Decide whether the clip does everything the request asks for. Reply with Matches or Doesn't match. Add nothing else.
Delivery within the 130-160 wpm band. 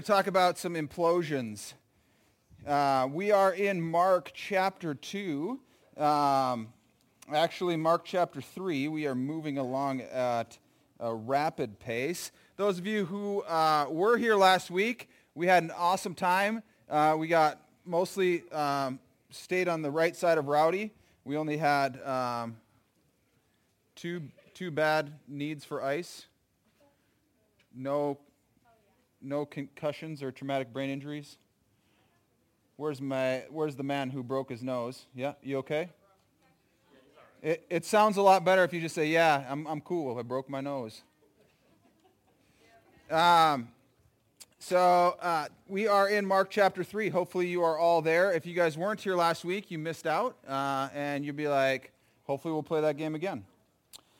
Matches